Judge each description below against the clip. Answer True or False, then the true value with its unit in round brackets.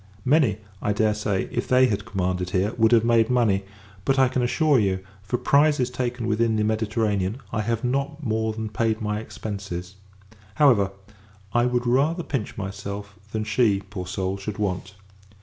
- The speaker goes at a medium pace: True (170 wpm)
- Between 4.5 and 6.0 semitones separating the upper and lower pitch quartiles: False (3.7 semitones)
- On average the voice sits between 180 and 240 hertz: False (110 Hz)